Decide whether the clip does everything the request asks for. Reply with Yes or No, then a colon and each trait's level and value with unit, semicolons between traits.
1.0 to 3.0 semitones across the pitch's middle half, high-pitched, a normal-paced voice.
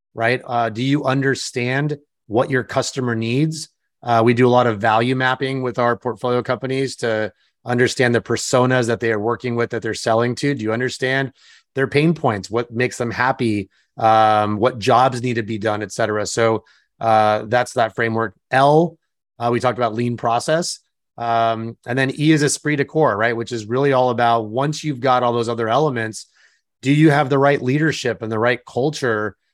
No: average, 2.7 semitones; low, 125 Hz; average, 195 wpm